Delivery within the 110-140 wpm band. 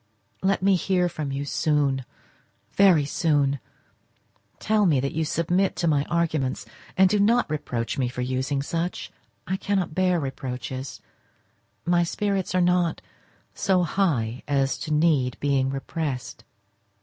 Yes: slow, 135 wpm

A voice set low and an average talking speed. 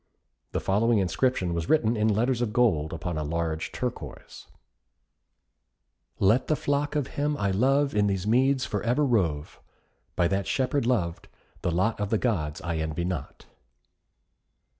Yes: low, 105 Hz; average, 155 wpm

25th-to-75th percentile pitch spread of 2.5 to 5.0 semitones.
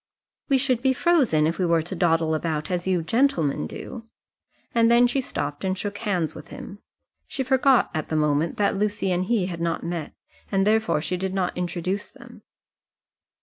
No: wide, 5.6 semitones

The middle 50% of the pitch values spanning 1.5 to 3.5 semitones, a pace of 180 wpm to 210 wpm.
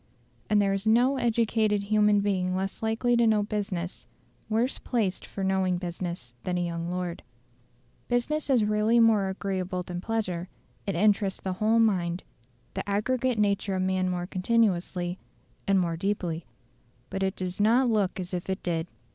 No: average, 3.2 semitones; average, 165 wpm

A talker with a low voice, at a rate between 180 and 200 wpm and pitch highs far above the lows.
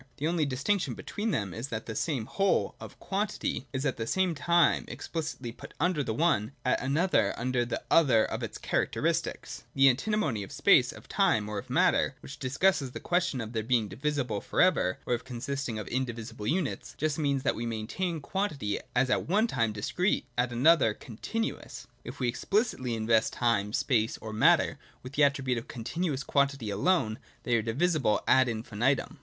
Yes: low, 130 Hz; average, 190 wpm; wide, 5.9 semitones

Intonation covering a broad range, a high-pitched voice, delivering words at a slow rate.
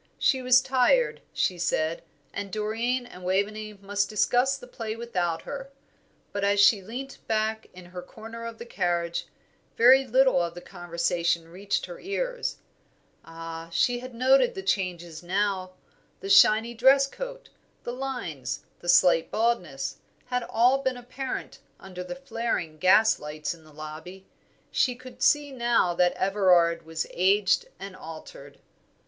No: wide, 6.1 semitones; high, 205 Hz; average, 150 wpm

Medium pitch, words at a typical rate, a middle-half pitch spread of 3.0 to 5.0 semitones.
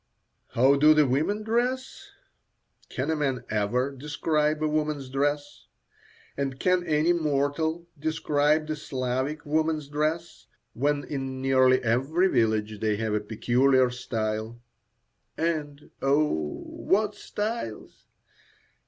No: medium, 145 Hz; slow, 115 wpm; average, 3.3 semitones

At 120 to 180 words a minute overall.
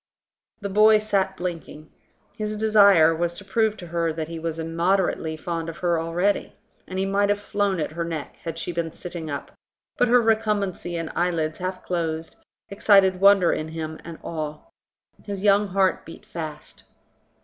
Yes: average, 170 wpm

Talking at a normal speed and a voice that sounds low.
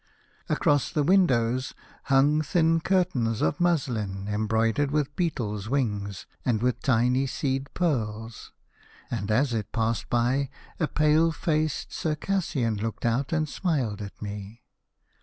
No: slow, 125 wpm; low, 130 Hz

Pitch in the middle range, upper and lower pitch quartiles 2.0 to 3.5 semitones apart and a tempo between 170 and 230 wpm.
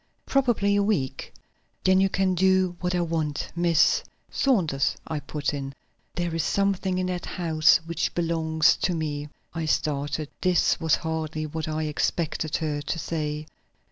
No: medium, 165 Hz; average, 3.1 semitones; average, 160 wpm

